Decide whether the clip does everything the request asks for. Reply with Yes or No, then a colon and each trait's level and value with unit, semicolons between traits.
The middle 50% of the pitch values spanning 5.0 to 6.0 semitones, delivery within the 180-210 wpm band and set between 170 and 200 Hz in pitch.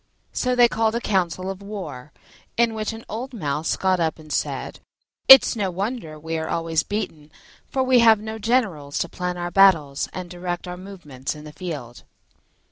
Yes: wide, 5.6 semitones; average, 185 wpm; medium, 185 Hz